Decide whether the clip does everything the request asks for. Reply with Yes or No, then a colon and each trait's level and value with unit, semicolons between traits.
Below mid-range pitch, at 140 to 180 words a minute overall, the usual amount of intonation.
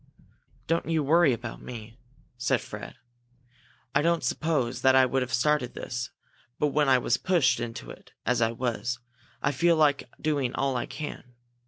Yes: low, 130 Hz; average, 170 wpm; average, 3.8 semitones